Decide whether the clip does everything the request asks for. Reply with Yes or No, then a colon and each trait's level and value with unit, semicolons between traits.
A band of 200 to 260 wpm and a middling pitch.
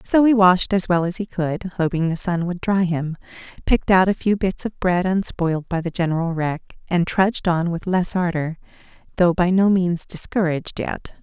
Yes: fast, 205 wpm; medium, 180 Hz